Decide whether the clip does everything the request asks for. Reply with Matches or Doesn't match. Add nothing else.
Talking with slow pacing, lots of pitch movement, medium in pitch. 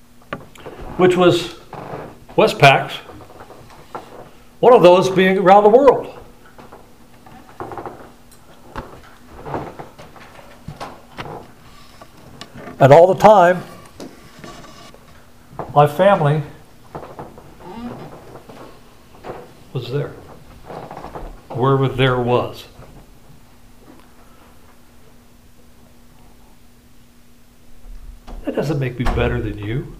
Matches